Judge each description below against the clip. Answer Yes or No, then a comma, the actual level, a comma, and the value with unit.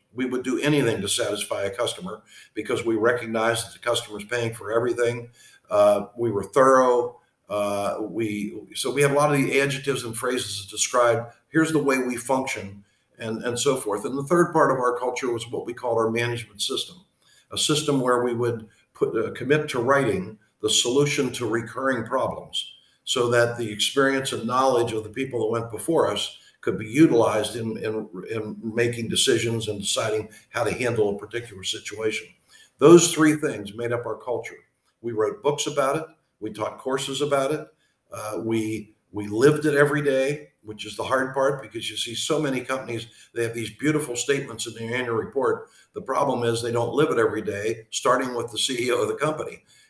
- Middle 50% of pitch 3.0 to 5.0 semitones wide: Yes, average, 3.5 semitones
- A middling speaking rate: Yes, average, 195 wpm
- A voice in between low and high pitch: No, low, 120 Hz